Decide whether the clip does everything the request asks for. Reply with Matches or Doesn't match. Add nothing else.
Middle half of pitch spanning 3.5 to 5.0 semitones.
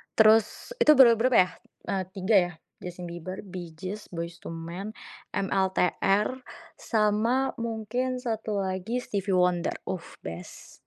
Matches